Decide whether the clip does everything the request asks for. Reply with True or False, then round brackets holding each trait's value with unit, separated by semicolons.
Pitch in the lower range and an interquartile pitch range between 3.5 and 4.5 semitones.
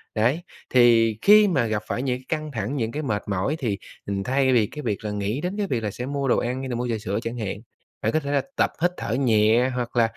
True (120 Hz; 4.2 semitones)